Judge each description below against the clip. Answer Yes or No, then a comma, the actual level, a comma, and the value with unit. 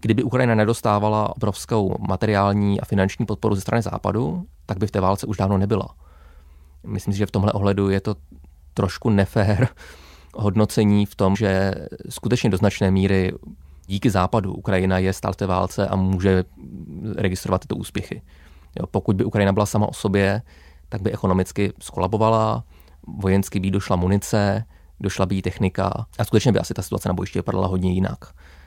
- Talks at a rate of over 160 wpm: Yes, fast, 170 wpm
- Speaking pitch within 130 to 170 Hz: No, low, 100 Hz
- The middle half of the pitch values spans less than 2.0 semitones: No, narrow, 2.5 semitones